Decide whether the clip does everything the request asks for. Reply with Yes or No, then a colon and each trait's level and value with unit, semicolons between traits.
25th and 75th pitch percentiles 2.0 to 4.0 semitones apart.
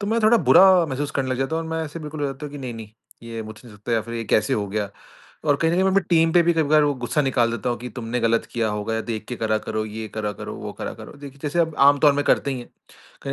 No: average, 5.1 semitones